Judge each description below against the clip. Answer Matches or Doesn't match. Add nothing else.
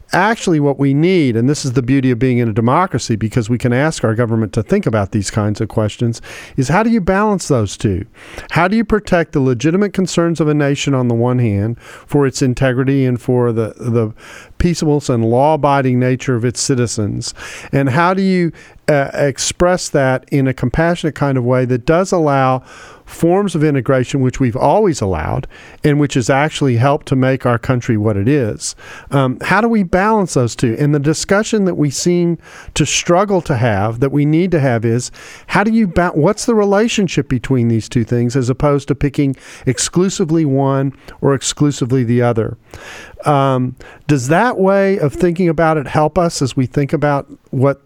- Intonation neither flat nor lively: Matches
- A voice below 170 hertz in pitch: Matches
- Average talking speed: Matches